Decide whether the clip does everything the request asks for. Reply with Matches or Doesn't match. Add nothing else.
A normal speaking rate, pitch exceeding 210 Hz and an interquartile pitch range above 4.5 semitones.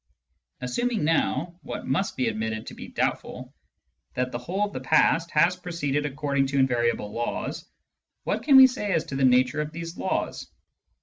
Doesn't match